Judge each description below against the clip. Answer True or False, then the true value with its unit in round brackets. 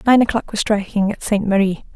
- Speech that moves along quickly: True (215 wpm)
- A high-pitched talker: True (210 Hz)